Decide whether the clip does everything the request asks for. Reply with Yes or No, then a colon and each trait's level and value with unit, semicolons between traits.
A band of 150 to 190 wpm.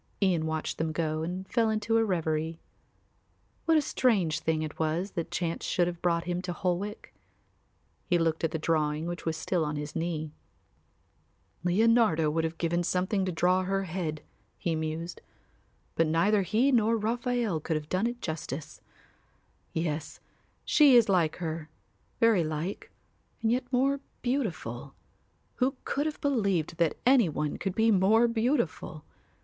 Yes: average, 160 wpm